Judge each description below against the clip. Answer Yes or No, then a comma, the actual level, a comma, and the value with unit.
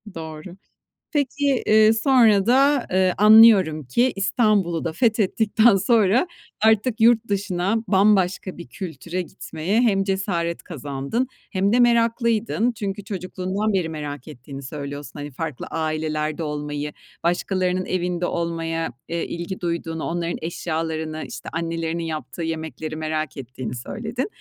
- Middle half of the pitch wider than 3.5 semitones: Yes, average, 5.2 semitones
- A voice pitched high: No, medium, 180 Hz